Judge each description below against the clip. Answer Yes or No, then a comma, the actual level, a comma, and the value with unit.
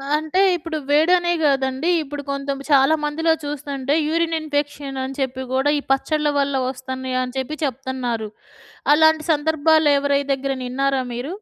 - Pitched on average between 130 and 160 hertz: No, very high, 280 Hz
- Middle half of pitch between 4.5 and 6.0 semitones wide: No, narrow, 2.6 semitones